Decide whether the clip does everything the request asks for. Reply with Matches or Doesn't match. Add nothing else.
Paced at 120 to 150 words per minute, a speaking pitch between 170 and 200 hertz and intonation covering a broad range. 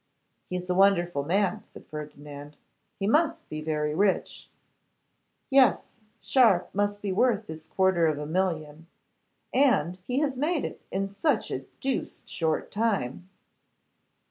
Matches